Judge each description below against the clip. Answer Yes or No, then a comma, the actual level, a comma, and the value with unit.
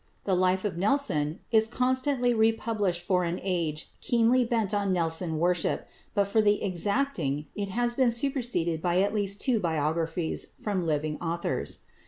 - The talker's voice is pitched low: No, high, 195 Hz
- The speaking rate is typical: Yes, average, 155 wpm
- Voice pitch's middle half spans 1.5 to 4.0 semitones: No, average, 5.1 semitones